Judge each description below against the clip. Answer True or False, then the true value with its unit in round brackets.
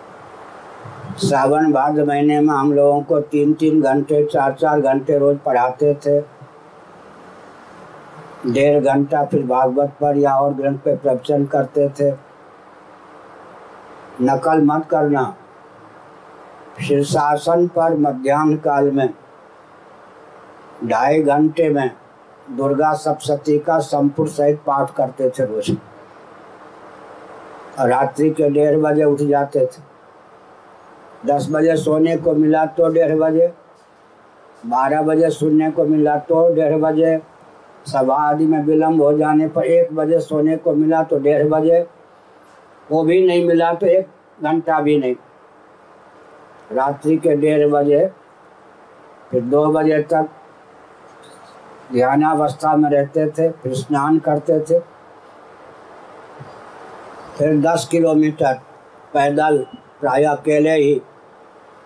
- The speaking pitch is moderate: True (150 Hz)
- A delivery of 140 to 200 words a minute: False (115 wpm)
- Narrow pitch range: True (2.1 semitones)